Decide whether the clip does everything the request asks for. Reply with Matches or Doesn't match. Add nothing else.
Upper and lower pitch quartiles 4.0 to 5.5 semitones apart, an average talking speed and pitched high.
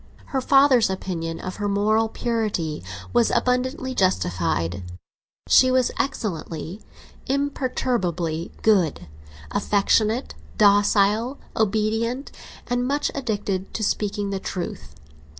Doesn't match